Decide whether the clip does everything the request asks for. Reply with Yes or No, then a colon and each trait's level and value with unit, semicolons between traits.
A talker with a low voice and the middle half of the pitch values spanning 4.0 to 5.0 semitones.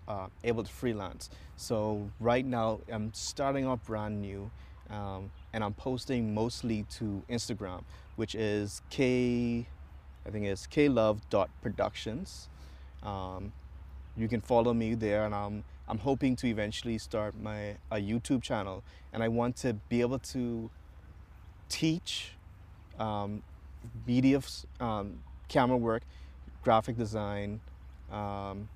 Yes: low, 105 Hz; average, 4.5 semitones